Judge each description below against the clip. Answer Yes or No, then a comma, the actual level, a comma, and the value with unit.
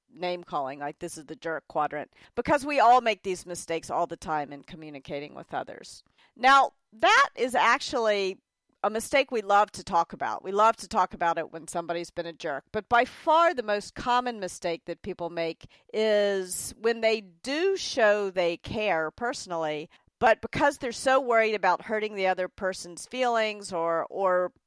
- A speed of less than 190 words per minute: Yes, average, 180 wpm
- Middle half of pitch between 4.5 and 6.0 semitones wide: Yes, wide, 5.6 semitones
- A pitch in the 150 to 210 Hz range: Yes, high, 190 Hz